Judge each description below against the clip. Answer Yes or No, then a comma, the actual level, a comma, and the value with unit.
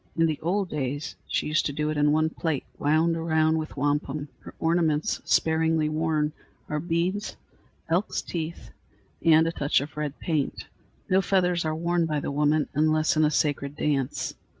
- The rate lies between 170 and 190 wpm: Yes, average, 175 wpm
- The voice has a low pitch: No, medium, 155 Hz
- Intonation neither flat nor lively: No, narrow, 1.8 semitones